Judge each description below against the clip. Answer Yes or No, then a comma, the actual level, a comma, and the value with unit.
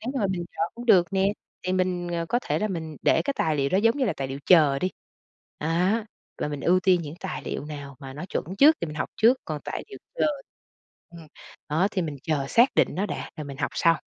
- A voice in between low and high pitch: Yes, medium, 175 Hz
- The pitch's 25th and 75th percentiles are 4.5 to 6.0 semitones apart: Yes, average, 5.0 semitones